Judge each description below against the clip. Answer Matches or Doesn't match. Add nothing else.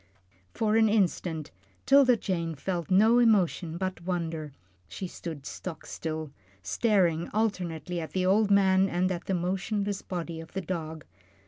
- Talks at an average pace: Matches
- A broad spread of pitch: Doesn't match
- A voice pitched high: Doesn't match